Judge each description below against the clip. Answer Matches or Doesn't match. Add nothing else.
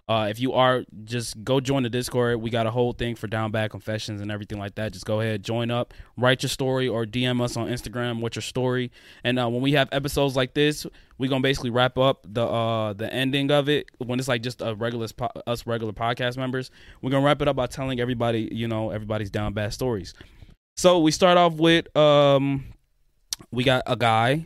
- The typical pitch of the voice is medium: Doesn't match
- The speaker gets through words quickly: Matches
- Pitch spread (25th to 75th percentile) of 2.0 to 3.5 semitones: Matches